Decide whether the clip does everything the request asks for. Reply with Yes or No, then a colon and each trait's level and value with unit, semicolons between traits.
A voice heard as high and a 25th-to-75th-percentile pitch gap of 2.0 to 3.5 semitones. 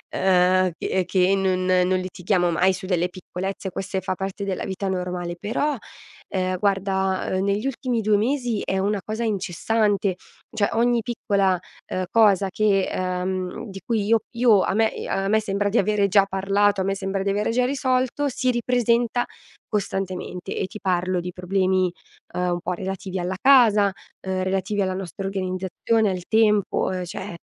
Yes: high, 195 Hz; narrow, 2.4 semitones